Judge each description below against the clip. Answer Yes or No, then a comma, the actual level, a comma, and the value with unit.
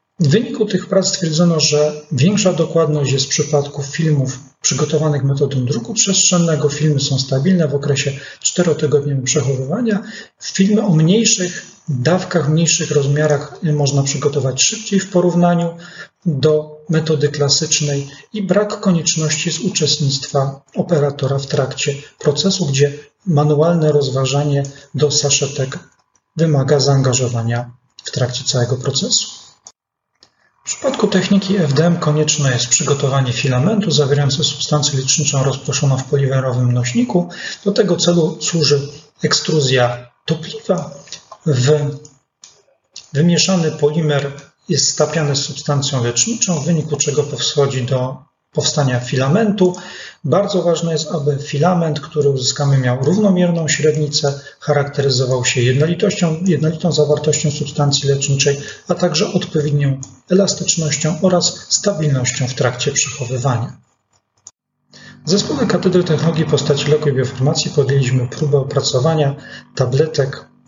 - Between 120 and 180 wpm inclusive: No, slow, 110 wpm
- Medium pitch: Yes, medium, 150 Hz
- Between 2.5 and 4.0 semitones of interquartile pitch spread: Yes, average, 3.4 semitones